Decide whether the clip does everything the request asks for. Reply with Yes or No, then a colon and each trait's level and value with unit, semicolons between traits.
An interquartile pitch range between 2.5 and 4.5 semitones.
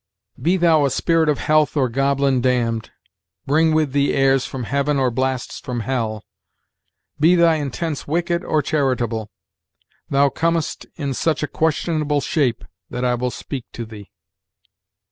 Yes: average, 3.7 semitones